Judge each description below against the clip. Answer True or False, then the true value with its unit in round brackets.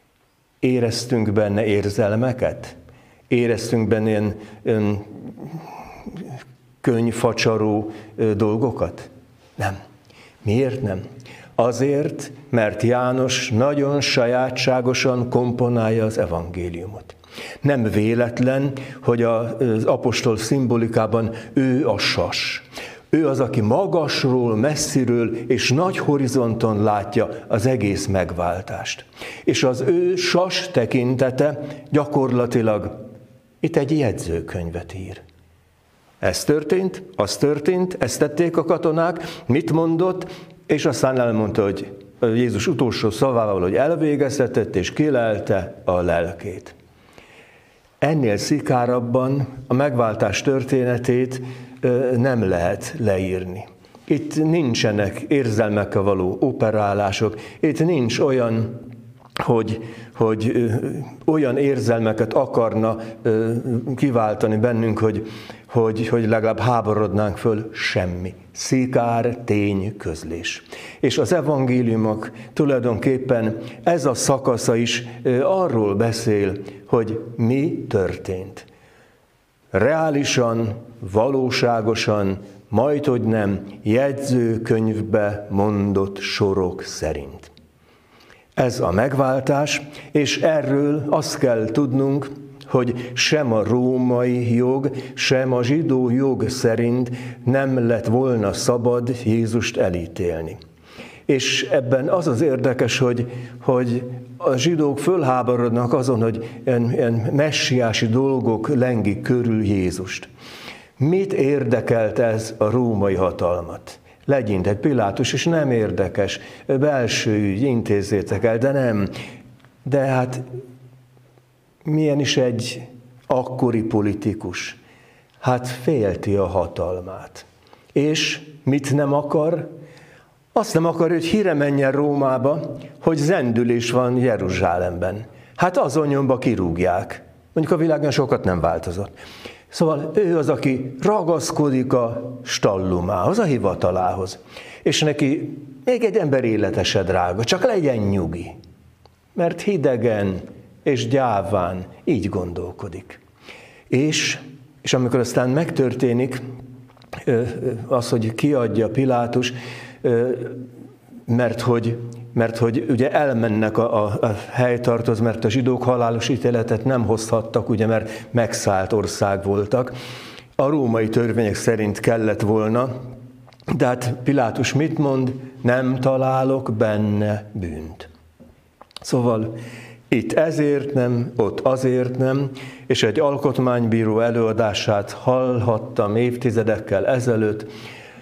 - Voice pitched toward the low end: True (120 Hz)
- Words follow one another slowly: True (100 wpm)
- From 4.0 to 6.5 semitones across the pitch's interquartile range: False (3.5 semitones)